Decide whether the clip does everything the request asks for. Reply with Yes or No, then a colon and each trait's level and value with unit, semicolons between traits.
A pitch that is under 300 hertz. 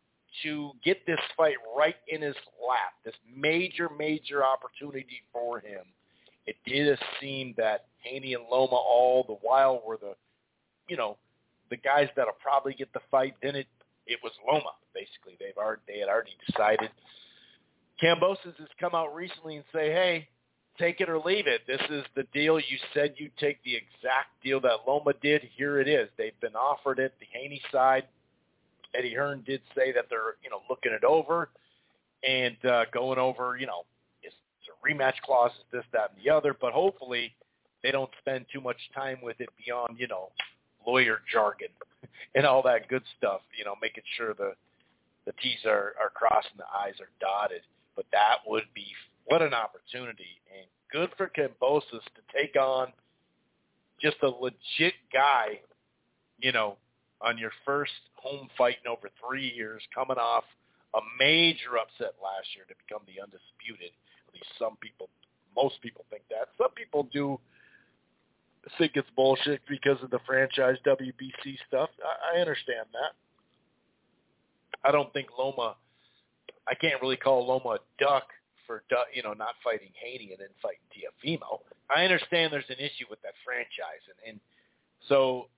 Yes: low, 135 Hz